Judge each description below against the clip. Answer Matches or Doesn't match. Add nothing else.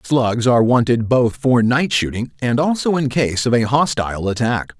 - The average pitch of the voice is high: Doesn't match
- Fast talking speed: Doesn't match